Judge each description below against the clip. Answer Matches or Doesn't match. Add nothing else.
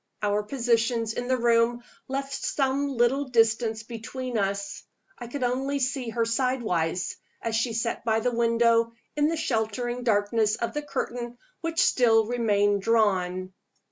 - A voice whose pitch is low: Doesn't match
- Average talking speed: Matches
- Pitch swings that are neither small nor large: Doesn't match